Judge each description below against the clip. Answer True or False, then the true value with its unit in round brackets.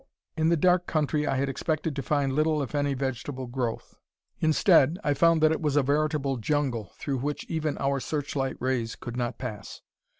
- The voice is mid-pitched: True (145 Hz)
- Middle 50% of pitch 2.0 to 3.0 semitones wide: True (2.7 semitones)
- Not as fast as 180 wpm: False (190 wpm)